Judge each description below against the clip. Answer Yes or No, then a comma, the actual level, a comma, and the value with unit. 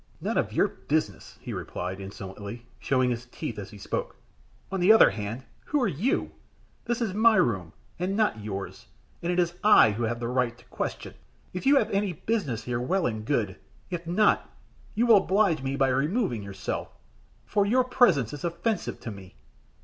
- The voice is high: No, medium, 140 Hz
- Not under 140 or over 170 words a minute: No, average, 190 wpm